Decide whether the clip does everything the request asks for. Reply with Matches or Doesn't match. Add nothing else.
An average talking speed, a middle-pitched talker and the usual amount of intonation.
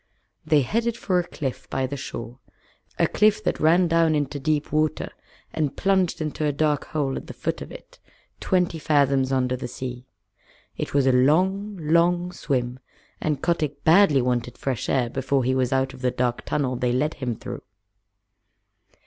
Matches